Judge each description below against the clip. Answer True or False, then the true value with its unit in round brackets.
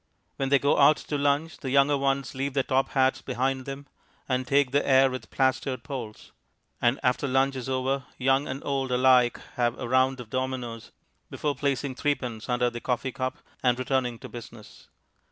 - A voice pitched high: False (130 Hz)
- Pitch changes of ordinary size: False (1.6 semitones)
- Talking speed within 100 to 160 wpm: False (185 wpm)